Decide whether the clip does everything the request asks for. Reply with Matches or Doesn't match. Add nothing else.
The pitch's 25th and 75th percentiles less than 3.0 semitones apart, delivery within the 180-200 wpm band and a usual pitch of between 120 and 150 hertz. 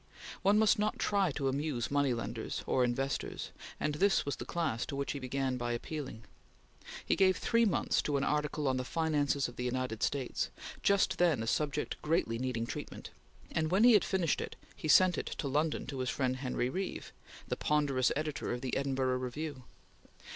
Doesn't match